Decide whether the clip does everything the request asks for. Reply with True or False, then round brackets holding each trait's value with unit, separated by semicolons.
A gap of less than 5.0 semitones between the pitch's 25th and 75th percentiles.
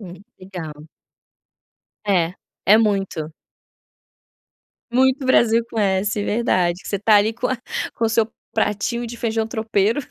True (3.2 semitones)